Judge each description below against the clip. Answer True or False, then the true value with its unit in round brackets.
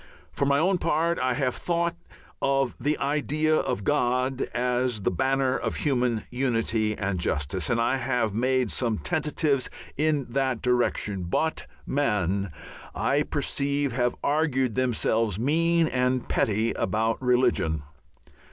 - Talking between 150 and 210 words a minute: False (135 wpm)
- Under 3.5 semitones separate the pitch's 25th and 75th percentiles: False (3.9 semitones)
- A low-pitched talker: True (130 Hz)